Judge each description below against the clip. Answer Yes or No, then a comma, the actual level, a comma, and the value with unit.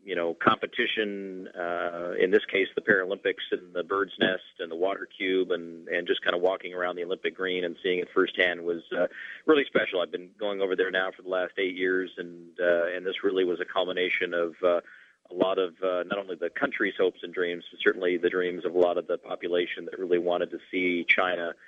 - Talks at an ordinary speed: No, fast, 230 wpm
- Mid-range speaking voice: No, very low, 90 Hz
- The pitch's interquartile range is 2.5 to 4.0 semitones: No, narrow, 1.3 semitones